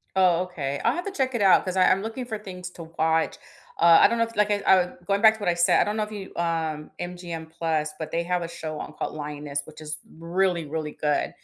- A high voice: No, medium, 175 Hz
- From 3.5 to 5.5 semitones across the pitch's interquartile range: Yes, average, 4.0 semitones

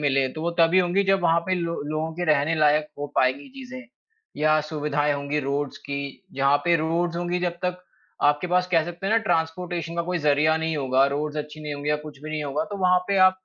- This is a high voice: No, medium, 155 Hz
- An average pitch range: Yes, average, 3.2 semitones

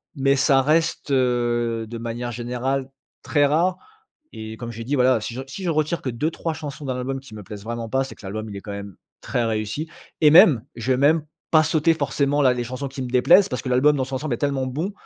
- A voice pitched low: Yes, low, 130 Hz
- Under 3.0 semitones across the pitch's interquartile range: No, average, 3.7 semitones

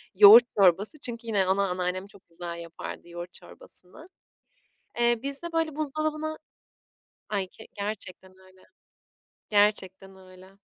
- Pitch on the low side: No, high, 200 Hz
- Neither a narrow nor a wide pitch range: Yes, average, 4.3 semitones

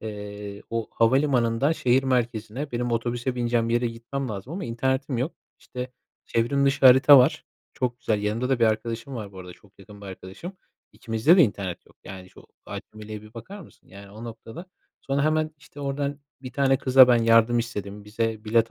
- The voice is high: No, low, 120 Hz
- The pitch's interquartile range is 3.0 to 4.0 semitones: Yes, average, 3.7 semitones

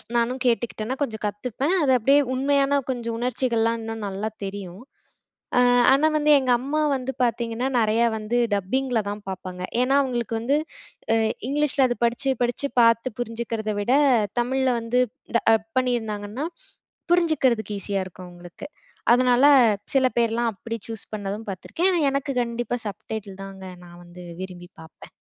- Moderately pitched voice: No, high, 235 Hz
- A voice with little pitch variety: No, average, 3.7 semitones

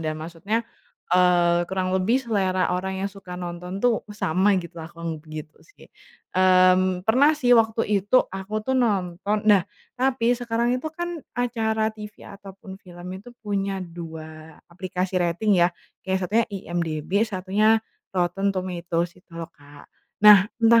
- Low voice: No, high, 190 Hz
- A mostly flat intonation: No, average, 3.8 semitones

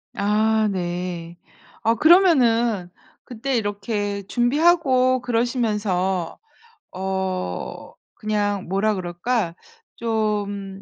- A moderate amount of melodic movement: Yes, average, 3.9 semitones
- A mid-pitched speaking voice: No, high, 210 Hz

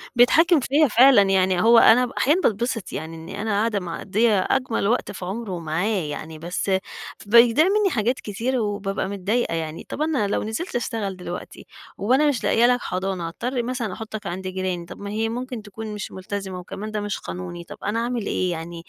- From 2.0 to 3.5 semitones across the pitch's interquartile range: No, average, 4.5 semitones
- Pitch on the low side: No, high, 210 Hz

